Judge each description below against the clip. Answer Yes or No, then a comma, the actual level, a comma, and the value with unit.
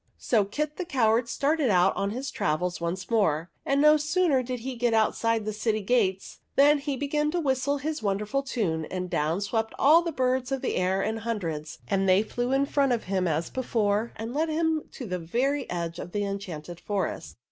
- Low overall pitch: No, high, 225 Hz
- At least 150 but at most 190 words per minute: No, fast, 205 wpm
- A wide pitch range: Yes, wide, 6.3 semitones